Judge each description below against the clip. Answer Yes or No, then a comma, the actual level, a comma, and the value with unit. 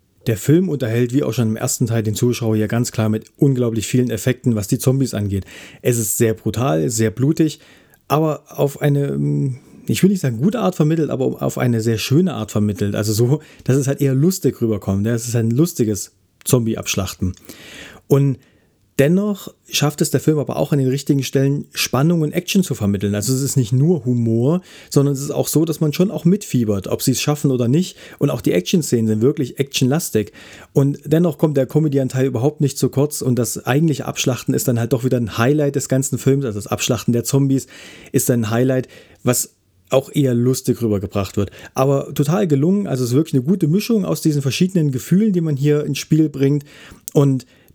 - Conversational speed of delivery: No, fast, 205 wpm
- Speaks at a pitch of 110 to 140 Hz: Yes, low, 135 Hz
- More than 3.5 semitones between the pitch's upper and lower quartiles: Yes, average, 4.4 semitones